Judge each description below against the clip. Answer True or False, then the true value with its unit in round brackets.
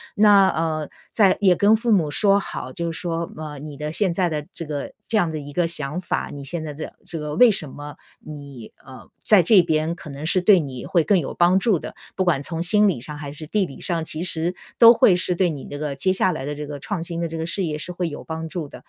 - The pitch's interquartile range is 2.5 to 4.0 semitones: True (3.6 semitones)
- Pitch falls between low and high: True (165 Hz)